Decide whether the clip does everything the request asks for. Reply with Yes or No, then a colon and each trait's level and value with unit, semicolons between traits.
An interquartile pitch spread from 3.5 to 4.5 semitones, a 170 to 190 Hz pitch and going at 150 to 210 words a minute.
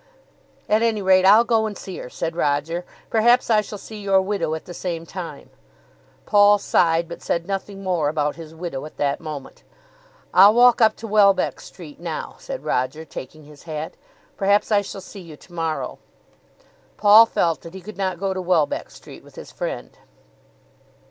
Yes: average, 4.2 semitones; medium, 185 Hz; average, 180 wpm